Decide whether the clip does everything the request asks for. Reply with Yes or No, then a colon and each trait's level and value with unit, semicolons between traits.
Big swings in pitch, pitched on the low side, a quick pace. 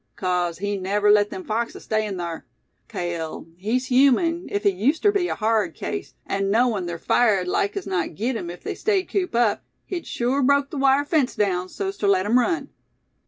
No: wide, 6.3 semitones; high, 215 Hz; fast, 210 wpm